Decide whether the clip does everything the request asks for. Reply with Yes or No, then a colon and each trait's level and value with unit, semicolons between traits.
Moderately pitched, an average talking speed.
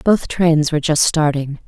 Yes: medium, 155 Hz; average, 180 wpm